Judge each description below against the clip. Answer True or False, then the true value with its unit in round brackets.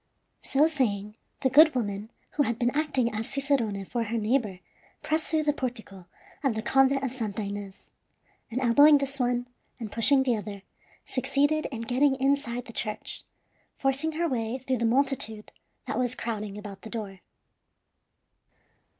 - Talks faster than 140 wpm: True (160 wpm)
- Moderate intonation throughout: True (4.1 semitones)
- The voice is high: True (245 Hz)